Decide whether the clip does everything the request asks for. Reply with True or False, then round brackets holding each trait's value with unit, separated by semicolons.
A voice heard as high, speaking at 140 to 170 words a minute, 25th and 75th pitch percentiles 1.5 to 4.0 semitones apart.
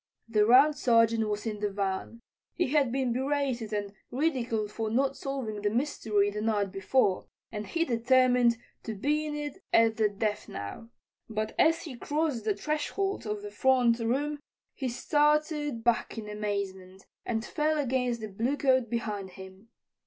False (230 Hz; 160 wpm; 4.5 semitones)